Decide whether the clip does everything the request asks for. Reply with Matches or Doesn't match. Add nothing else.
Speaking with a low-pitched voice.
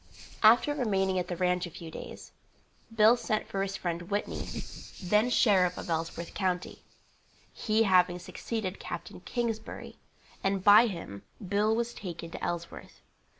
Doesn't match